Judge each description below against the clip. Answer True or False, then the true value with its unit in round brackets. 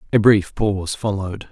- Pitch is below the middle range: True (100 Hz)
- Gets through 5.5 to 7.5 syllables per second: True (5.6 syllables/s)